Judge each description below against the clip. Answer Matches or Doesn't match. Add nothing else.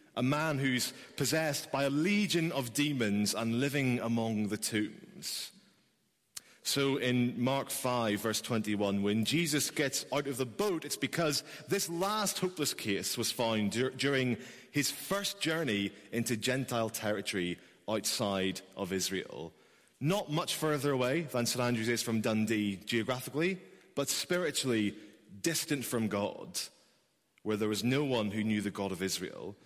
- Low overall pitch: Matches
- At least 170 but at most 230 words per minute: Doesn't match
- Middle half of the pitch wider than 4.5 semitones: Matches